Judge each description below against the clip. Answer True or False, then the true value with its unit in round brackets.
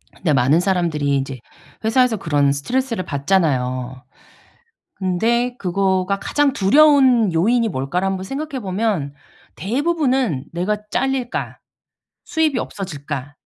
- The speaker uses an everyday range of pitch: False (9.0 semitones)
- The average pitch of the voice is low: False (190 Hz)